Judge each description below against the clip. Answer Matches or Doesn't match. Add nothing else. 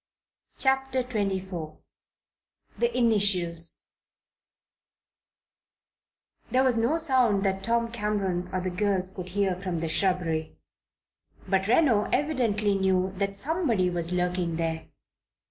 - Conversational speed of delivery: Doesn't match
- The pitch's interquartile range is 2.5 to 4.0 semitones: Doesn't match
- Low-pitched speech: Doesn't match